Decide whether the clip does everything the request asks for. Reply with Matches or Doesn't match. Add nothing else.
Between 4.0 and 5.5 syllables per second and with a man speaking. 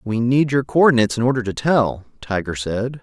Doesn't match